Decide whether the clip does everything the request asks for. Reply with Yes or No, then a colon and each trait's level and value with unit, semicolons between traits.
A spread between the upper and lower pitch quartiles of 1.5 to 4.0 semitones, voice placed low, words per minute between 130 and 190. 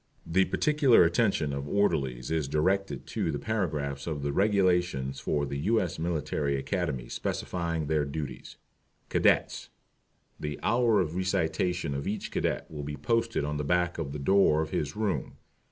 No: average, 4.8 semitones; very low, 80 Hz; average, 160 wpm